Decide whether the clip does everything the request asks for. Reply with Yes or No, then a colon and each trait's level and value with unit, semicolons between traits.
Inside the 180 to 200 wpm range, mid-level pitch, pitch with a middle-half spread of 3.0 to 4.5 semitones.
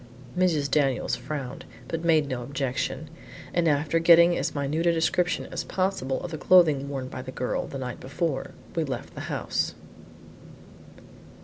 No: average, 155 wpm; medium, 150 Hz; average, 3.8 semitones